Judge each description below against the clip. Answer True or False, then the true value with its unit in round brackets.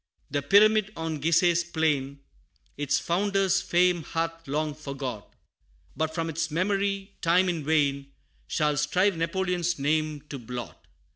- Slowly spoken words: True (130 wpm)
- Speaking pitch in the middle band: True (165 Hz)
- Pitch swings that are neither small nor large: True (3.7 semitones)